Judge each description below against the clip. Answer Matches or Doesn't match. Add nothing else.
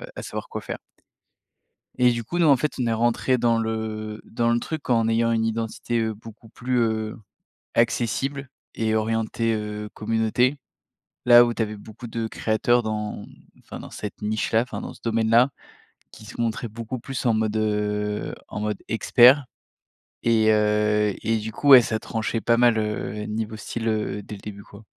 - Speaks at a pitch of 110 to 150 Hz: Matches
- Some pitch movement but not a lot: Doesn't match